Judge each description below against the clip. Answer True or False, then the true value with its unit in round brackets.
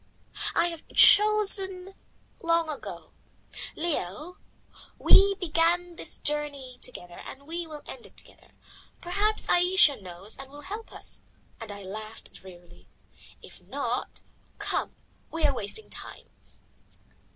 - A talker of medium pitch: False (315 Hz)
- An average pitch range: False (7.0 semitones)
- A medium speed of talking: False (120 wpm)